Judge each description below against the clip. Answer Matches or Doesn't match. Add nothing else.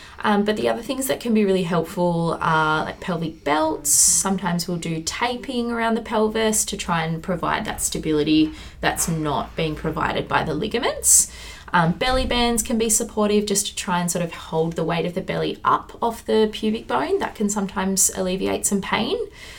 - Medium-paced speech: Matches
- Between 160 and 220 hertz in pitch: Matches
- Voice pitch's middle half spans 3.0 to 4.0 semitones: Doesn't match